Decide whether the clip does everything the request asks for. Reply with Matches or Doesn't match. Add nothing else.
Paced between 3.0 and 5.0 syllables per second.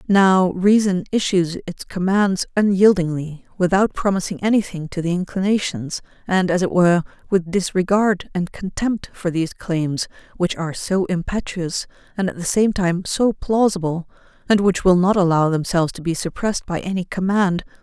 Matches